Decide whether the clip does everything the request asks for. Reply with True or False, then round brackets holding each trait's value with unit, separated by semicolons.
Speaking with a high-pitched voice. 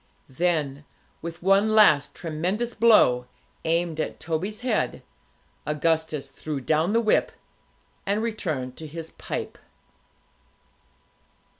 False (165 Hz)